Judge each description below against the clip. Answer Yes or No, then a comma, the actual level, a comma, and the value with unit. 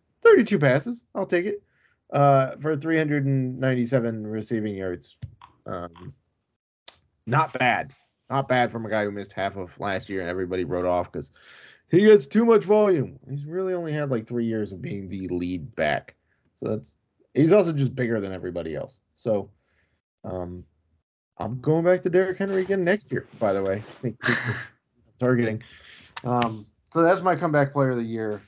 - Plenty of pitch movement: Yes, wide, 8.6 semitones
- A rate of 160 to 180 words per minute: Yes, average, 165 wpm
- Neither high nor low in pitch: No, low, 120 Hz